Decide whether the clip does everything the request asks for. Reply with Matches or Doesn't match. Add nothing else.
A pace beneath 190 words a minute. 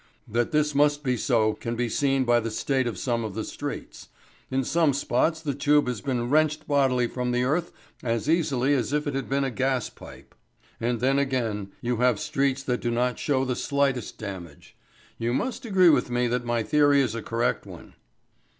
Doesn't match